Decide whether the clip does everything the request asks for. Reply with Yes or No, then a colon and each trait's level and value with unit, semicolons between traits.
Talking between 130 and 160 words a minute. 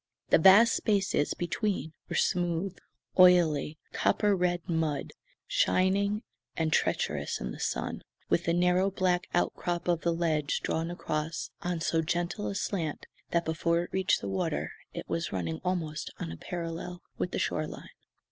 Yes: average, 155 wpm